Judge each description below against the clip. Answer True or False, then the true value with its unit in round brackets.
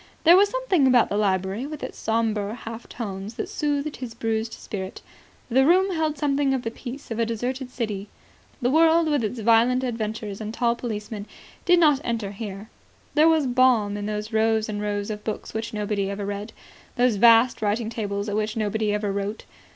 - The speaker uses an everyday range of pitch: True (3.7 semitones)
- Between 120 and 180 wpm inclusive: False (190 wpm)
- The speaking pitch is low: False (225 Hz)